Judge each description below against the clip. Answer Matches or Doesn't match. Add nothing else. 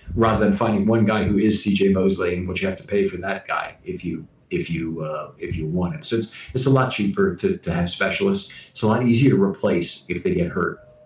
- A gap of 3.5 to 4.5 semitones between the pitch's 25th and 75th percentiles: Doesn't match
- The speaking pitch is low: Matches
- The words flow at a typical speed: Doesn't match